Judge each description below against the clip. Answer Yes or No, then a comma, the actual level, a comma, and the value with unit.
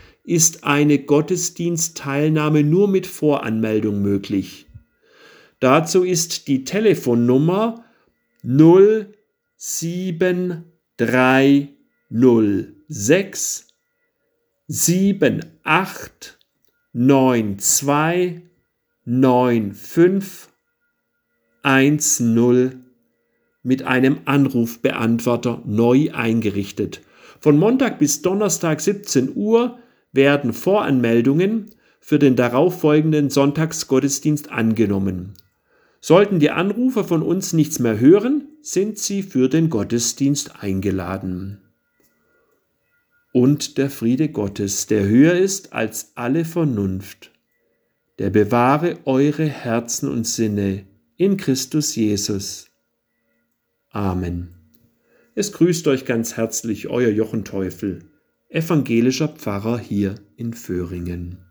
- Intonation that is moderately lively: No, wide, 7.1 semitones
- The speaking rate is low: Yes, slow, 80 wpm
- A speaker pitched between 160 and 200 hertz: No, low, 135 Hz